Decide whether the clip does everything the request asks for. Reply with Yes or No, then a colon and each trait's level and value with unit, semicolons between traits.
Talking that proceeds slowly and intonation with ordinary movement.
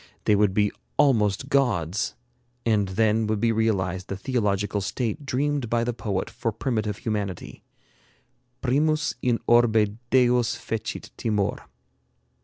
Yes: slow, 125 wpm; average, 3.0 semitones